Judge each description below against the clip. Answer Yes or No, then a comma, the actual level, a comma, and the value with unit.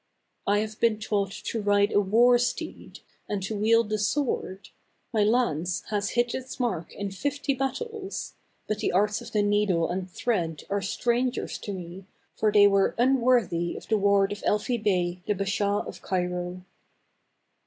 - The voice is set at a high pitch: Yes, high, 205 Hz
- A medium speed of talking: Yes, average, 175 wpm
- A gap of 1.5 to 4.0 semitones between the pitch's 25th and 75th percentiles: Yes, average, 3.5 semitones